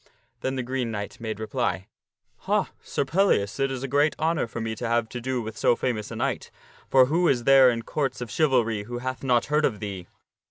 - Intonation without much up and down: No, average, 3.3 semitones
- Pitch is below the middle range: Yes, low, 125 Hz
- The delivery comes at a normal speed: No, fast, 230 wpm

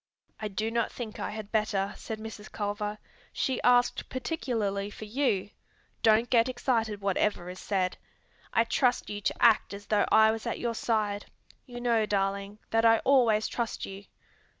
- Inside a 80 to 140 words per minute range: No, average, 170 wpm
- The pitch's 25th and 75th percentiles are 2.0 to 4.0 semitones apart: Yes, narrow, 2.4 semitones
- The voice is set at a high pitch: Yes, high, 220 Hz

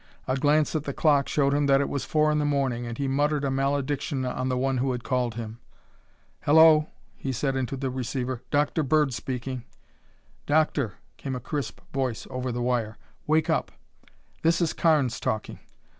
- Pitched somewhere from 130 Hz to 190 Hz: Yes, low, 135 Hz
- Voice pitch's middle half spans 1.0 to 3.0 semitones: Yes, narrow, 2.6 semitones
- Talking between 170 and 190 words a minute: Yes, average, 185 wpm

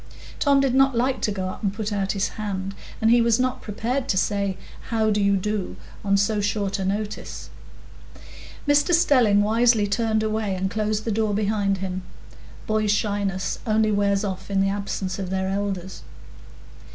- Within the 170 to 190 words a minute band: Yes, average, 175 wpm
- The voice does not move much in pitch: Yes, narrow, 2.0 semitones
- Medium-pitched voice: No, high, 205 Hz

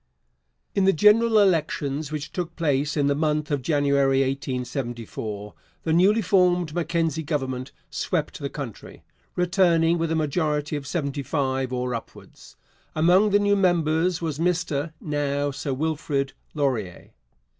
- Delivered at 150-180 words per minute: No, slow, 135 wpm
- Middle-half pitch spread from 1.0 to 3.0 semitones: No, average, 3.7 semitones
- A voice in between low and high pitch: Yes, medium, 150 Hz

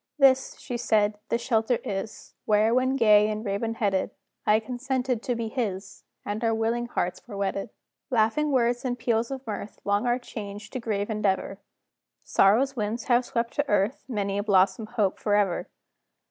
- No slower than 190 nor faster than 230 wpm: No, average, 170 wpm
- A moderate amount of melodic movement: Yes, average, 3.0 semitones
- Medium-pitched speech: No, high, 225 Hz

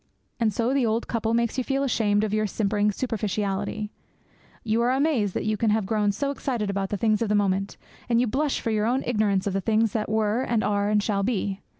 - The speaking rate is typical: No, fast, 235 wpm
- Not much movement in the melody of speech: Yes, narrow, 2.3 semitones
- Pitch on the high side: Yes, high, 215 Hz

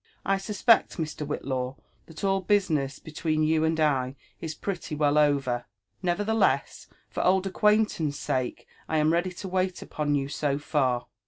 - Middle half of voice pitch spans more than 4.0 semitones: Yes, average, 4.7 semitones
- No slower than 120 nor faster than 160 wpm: Yes, average, 155 wpm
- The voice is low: No, medium, 155 Hz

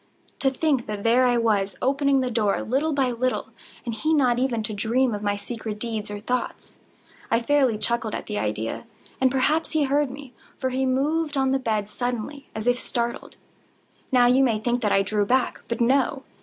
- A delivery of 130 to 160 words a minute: No, average, 195 wpm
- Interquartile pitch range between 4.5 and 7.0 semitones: No, average, 3.5 semitones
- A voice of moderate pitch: No, high, 245 Hz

